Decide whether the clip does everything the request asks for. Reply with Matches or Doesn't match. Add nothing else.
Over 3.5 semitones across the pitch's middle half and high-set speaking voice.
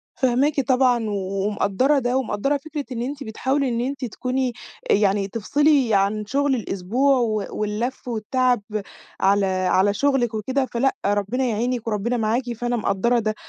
Matches